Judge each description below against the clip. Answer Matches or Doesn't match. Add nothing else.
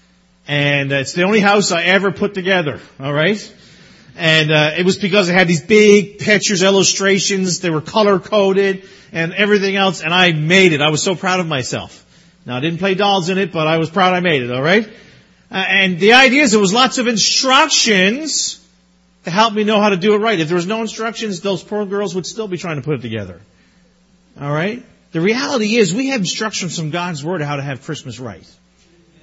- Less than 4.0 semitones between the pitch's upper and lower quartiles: Doesn't match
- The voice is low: Doesn't match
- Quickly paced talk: Matches